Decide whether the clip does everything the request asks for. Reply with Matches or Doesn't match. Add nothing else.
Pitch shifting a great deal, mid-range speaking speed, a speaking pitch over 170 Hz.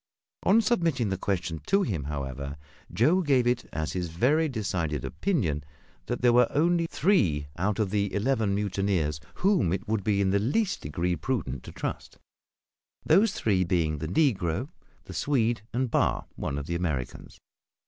Doesn't match